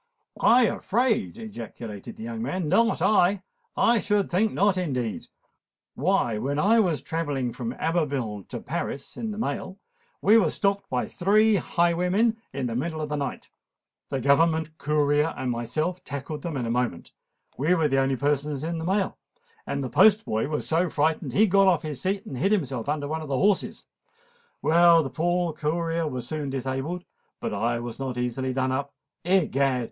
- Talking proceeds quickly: No, average, 180 wpm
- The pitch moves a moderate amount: No, wide, 5.9 semitones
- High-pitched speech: No, medium, 155 Hz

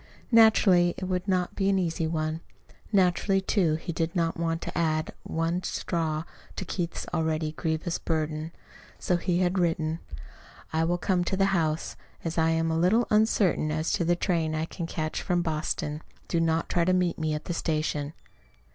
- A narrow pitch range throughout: Yes, narrow, 2.2 semitones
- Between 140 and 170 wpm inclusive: No, average, 180 wpm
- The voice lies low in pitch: No, medium, 165 Hz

